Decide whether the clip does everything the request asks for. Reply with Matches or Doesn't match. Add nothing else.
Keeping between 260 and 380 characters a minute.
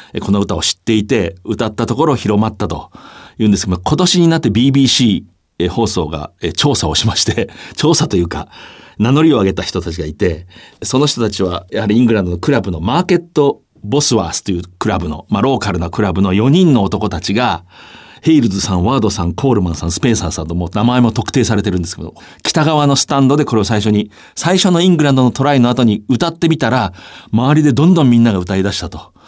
Doesn't match